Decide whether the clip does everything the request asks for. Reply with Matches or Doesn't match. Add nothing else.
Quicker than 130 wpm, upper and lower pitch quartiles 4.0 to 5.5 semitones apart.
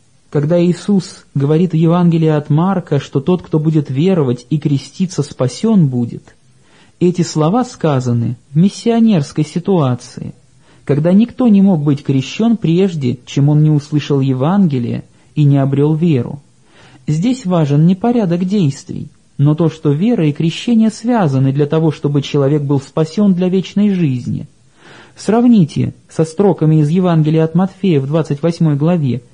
Matches